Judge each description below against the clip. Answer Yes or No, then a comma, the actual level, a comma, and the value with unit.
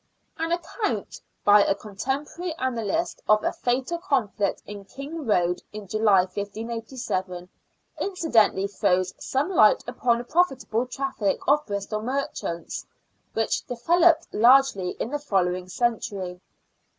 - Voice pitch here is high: Yes, high, 230 Hz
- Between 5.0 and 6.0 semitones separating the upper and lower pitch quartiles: Yes, wide, 5.6 semitones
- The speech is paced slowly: Yes, slow, 115 wpm